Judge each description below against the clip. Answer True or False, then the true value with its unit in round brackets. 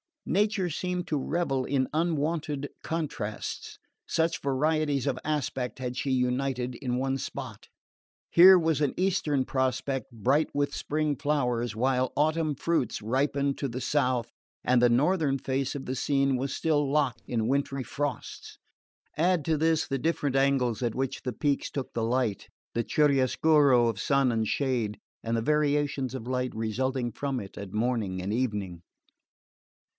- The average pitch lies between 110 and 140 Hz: True (135 Hz)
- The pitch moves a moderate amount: True (3.2 semitones)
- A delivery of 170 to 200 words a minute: False (150 wpm)